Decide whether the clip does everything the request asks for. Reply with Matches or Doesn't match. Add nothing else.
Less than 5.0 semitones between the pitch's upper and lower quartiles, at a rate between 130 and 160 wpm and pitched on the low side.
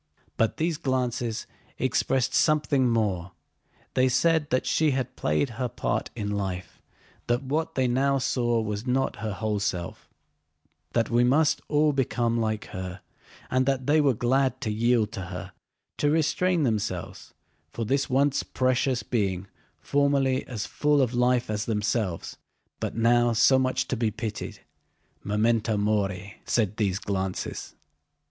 Matches